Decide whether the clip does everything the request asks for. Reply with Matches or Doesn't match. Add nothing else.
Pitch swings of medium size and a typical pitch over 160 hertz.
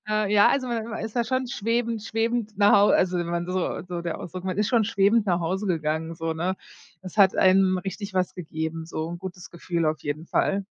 Matches